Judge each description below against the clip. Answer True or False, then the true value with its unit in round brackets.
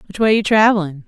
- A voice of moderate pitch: False (200 Hz)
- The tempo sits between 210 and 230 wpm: True (225 wpm)